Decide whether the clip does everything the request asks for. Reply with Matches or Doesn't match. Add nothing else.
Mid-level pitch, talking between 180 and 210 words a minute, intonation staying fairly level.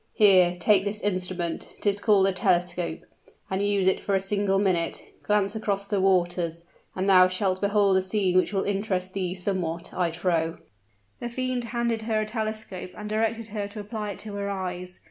Doesn't match